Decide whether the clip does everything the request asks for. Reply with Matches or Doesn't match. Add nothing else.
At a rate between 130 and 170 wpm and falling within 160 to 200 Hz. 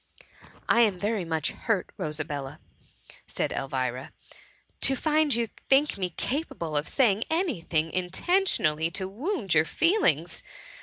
Matches